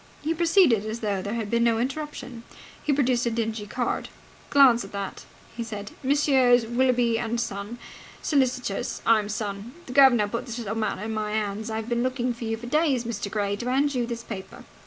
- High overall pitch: Yes, high, 235 Hz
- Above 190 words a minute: Yes, average, 200 wpm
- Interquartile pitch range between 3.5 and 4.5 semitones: No, average, 2.7 semitones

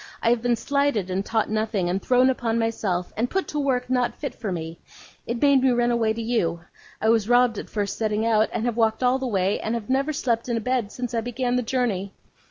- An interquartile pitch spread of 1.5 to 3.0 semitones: Yes, narrow, 2.6 semitones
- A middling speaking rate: No, fast, 245 wpm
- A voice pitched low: No, high, 230 Hz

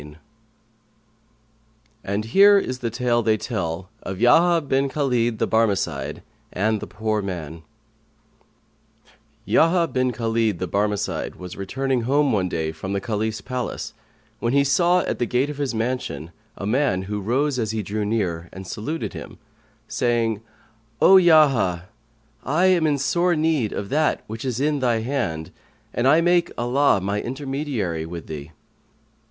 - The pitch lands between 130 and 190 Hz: No, low, 115 Hz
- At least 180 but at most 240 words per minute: No, average, 155 wpm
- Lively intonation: Yes, wide, 5.8 semitones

